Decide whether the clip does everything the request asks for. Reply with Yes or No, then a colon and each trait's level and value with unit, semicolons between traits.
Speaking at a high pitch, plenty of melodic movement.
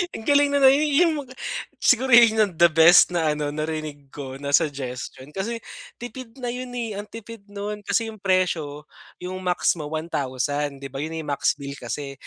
No: medium, 175 Hz; wide, 7.9 semitones